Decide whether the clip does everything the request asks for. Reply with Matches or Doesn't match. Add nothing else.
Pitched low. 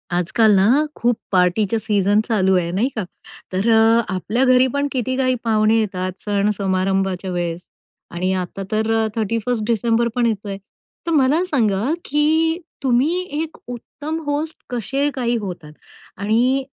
Doesn't match